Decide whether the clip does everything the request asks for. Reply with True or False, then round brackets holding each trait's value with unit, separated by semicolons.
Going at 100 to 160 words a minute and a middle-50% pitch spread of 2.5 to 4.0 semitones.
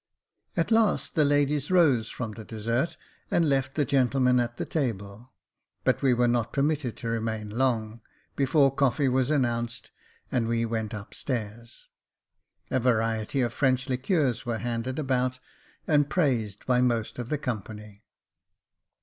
True (150 wpm; 3.2 semitones)